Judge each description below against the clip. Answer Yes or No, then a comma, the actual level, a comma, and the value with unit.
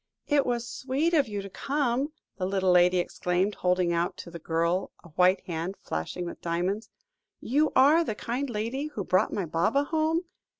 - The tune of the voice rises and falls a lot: Yes, wide, 7.4 semitones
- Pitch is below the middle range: No, high, 200 Hz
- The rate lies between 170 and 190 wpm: Yes, average, 180 wpm